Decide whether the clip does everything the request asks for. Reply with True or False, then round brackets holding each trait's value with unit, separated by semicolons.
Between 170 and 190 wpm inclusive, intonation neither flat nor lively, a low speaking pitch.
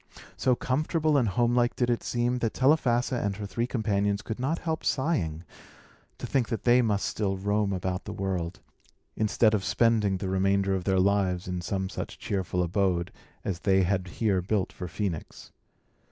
True (175 wpm; 4.1 semitones; 100 Hz)